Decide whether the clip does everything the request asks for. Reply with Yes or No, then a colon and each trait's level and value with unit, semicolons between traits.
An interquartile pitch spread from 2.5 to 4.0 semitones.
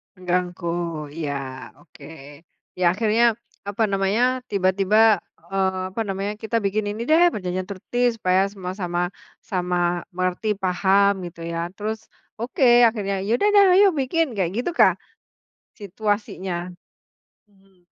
Yes: average, 2.9 semitones